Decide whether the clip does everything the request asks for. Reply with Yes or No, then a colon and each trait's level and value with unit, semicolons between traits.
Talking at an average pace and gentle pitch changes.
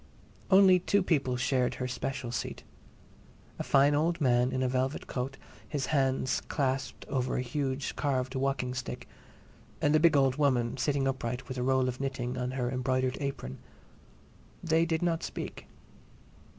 Yes: average, 160 wpm; narrow, 2.2 semitones